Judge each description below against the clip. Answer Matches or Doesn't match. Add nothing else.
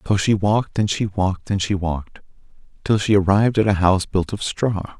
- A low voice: Matches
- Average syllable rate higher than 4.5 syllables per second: Matches